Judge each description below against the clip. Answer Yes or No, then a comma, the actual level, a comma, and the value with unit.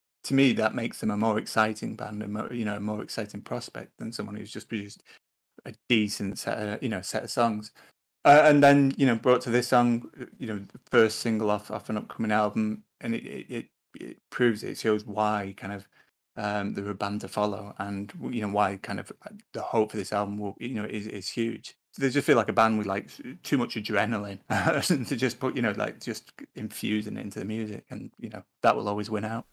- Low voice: Yes, low, 110 Hz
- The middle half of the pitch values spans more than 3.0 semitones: No, narrow, 2.6 semitones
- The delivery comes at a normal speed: No, fast, 235 wpm